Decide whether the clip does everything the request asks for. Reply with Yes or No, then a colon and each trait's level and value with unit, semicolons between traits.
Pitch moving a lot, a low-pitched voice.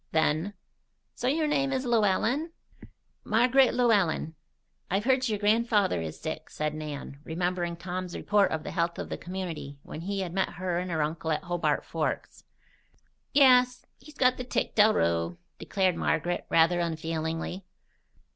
No: wide, 6.3 semitones; medium, 185 Hz